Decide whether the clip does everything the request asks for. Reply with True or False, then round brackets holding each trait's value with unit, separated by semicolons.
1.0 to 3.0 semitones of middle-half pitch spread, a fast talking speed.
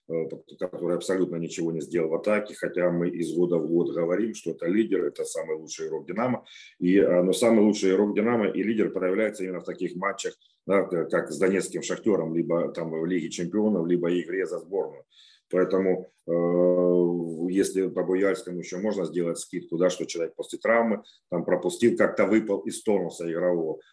False (3.8 semitones; 175 wpm)